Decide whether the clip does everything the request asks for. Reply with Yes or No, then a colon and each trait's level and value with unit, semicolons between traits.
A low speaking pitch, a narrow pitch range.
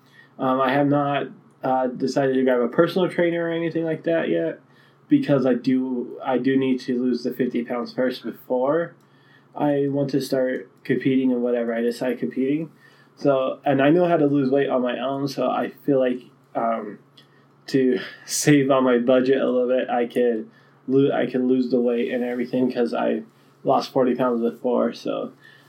Yes: low, 130 Hz; narrow, 2.1 semitones